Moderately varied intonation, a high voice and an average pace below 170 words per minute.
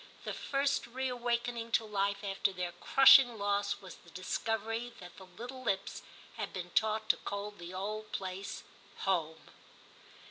Yes: average, 3.7 semitones; high, 205 Hz; average, 150 wpm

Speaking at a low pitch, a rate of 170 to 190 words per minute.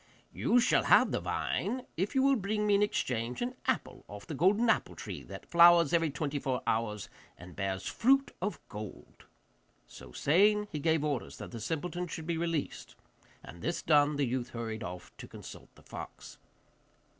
No: medium, 160 Hz; average, 180 wpm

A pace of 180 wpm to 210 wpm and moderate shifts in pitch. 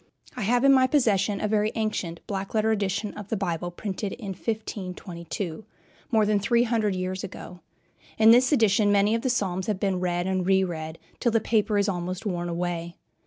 Yes: average, 195 wpm; average, 3.3 semitones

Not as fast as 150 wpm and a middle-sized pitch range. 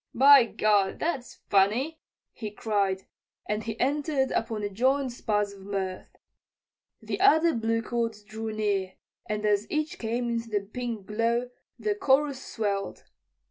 Yes: average, 140 wpm; average, 4.1 semitones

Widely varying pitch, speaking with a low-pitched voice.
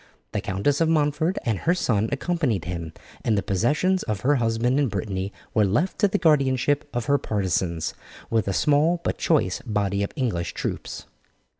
Yes: wide, 6.8 semitones; low, 120 Hz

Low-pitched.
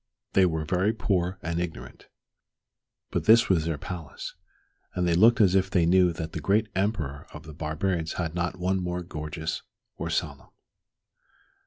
Yes: very low, 90 Hz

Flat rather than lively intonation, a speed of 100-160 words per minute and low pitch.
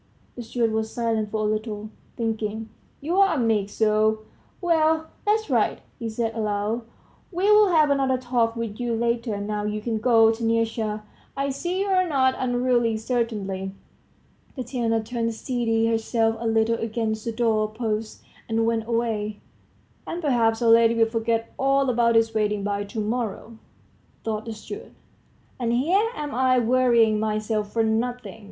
No: narrow, 2.3 semitones; average, 150 wpm; high, 230 Hz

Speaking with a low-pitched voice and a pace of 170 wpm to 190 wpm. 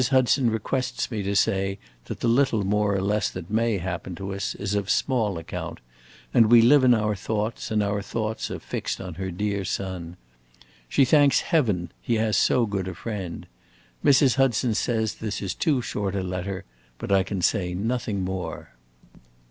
Yes: low, 105 Hz; average, 185 wpm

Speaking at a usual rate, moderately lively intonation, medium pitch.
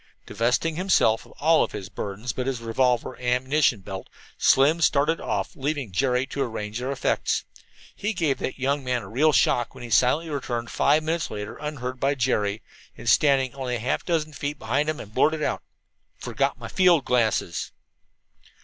No: average, 175 wpm; average, 4.1 semitones; low, 130 Hz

